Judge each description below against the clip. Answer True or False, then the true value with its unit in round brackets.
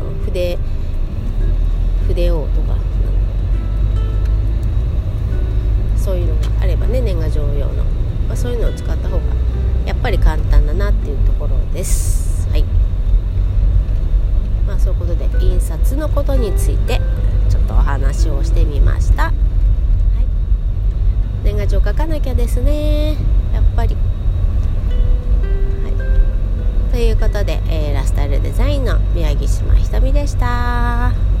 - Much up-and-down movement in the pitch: False (2.3 semitones)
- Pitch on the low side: True (95 Hz)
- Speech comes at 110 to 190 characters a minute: False (240 characters per minute)